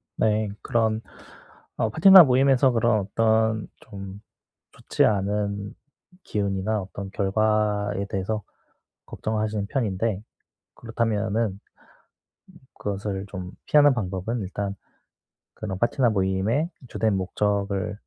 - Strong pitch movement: No, narrow, 2.3 semitones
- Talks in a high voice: No, low, 105 Hz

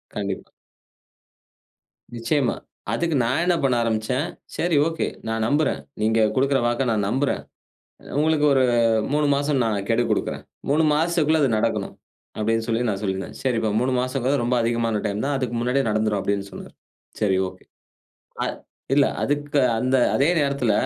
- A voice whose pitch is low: Yes, low, 125 Hz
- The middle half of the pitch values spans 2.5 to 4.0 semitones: No, average, 4.6 semitones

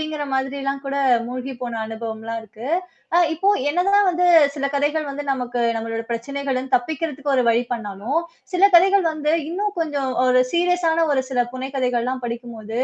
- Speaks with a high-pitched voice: Yes, very high, 270 Hz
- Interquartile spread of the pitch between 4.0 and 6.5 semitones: Yes, average, 4.6 semitones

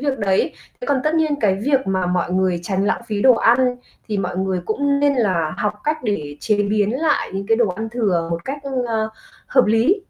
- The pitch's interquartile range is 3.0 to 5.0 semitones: No, wide, 5.6 semitones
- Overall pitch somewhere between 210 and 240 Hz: Yes, high, 215 Hz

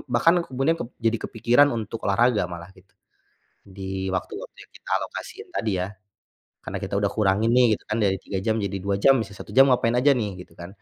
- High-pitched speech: No, low, 105 Hz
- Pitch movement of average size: Yes, average, 3.9 semitones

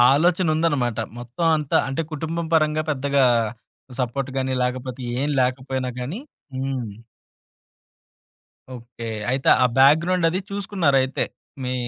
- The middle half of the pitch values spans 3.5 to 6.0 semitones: Yes, average, 4.0 semitones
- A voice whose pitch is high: No, low, 135 Hz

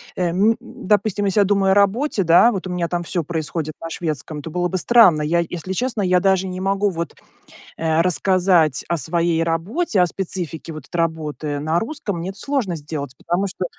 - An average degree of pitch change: Yes, average, 3.1 semitones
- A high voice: No, medium, 180 Hz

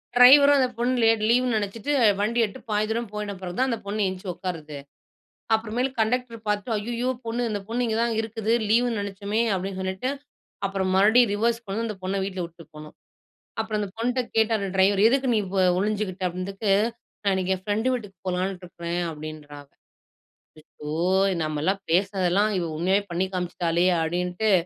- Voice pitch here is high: Yes, high, 205 Hz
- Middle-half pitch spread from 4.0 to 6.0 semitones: No, average, 3.6 semitones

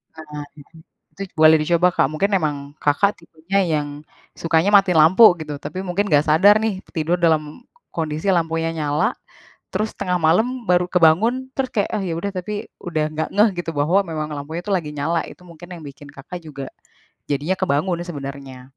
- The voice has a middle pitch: Yes, medium, 165 Hz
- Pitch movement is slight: No, average, 3.6 semitones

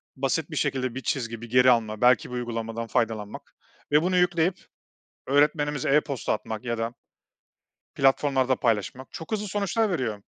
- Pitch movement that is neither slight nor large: Yes, average, 4.4 semitones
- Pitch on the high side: No, low, 130 Hz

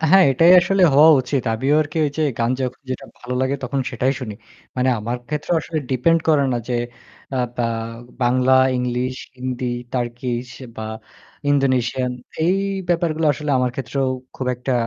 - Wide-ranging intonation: No, average, 3.3 semitones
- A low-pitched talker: Yes, low, 130 Hz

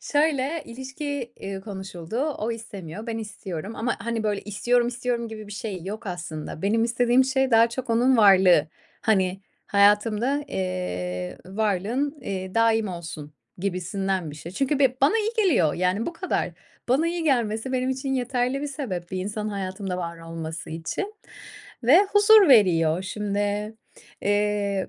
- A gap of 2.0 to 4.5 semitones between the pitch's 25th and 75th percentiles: No, average, 5.3 semitones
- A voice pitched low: No, high, 215 Hz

